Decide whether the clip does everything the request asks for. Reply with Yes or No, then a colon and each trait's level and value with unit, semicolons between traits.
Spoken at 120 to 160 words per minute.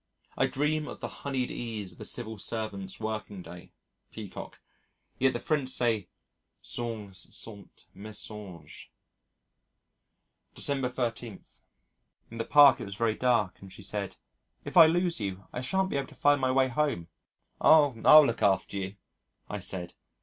Yes: average, 155 wpm